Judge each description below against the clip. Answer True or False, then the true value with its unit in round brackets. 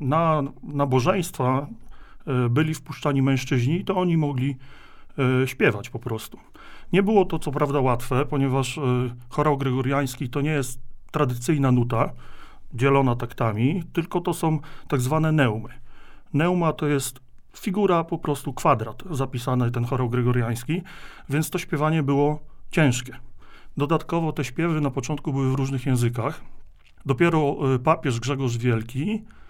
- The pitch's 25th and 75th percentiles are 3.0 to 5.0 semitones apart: True (3.8 semitones)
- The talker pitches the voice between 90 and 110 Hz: False (140 Hz)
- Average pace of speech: True (125 wpm)